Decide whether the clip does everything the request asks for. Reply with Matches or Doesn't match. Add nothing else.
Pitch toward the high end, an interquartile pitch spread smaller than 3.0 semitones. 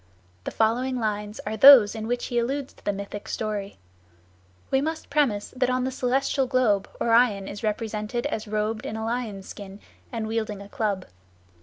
Doesn't match